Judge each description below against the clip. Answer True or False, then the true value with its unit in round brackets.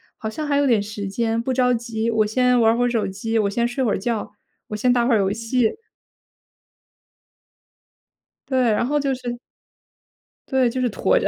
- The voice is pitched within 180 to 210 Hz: False (235 Hz)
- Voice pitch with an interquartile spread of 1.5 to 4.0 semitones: True (2.5 semitones)